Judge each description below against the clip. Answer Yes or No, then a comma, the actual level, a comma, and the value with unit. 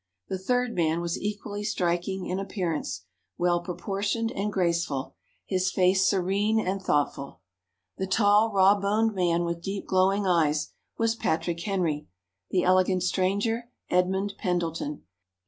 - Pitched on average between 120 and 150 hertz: No, medium, 185 Hz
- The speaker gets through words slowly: Yes, slow, 130 wpm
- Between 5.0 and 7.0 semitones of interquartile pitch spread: No, average, 2.9 semitones